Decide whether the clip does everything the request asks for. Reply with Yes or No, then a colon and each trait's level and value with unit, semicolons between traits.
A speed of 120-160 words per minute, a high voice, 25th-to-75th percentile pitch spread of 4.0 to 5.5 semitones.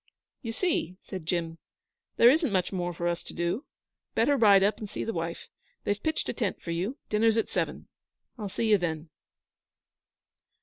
No: average, 180 wpm; high, 200 Hz; average, 4.7 semitones